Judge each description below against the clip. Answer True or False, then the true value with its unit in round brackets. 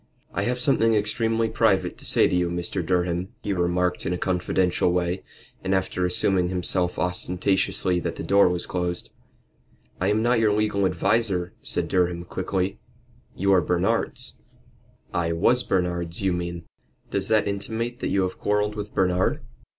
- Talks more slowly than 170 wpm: True (160 wpm)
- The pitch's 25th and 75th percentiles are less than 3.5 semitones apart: True (2.7 semitones)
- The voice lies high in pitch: False (95 Hz)